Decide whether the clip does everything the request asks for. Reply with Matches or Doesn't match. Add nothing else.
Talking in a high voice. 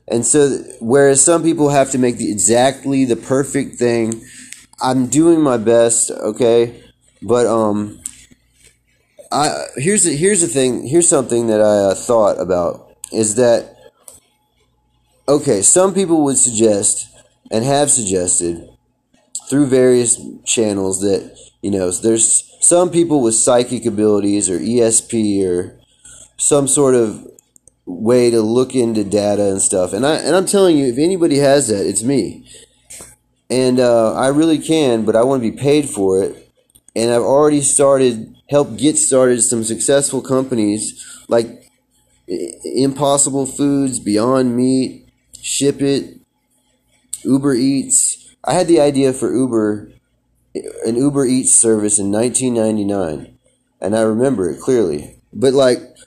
Doesn't match